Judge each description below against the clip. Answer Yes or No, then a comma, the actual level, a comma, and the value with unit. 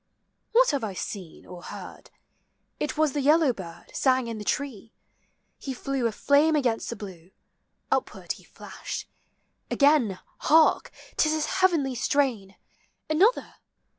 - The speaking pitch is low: No, very high, 270 Hz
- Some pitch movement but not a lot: No, wide, 6.1 semitones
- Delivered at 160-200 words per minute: No, average, 140 wpm